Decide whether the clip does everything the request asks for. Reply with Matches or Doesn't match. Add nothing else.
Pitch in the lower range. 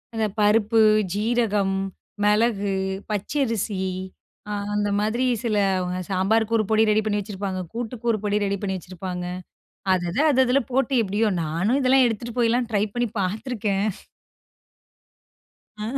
Doesn't match